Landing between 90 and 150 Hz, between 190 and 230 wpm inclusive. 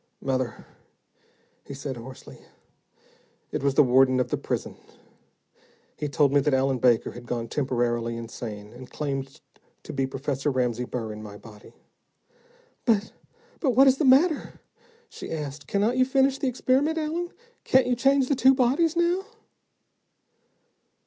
No: medium, 140 Hz; average, 150 wpm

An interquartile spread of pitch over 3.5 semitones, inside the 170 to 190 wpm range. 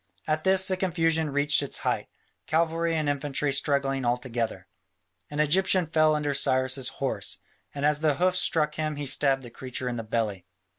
No: average, 3.1 semitones; average, 180 wpm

